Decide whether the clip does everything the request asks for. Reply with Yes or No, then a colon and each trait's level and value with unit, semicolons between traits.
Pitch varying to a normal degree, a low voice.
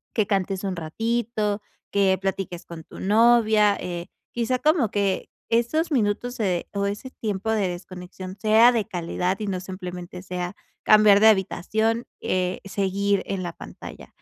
No: average, 3.0 semitones; high, 200 Hz